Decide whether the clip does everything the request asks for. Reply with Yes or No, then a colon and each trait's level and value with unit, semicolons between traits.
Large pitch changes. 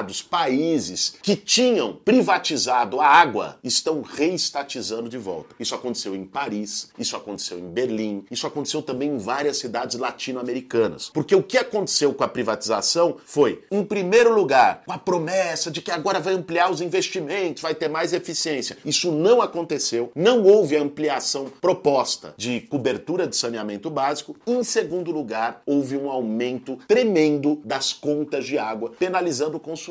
Yes: wide, 6.0 semitones